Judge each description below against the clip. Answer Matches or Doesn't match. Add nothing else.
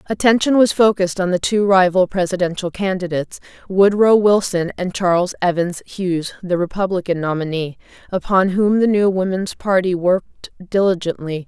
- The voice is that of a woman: Matches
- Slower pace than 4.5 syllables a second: Doesn't match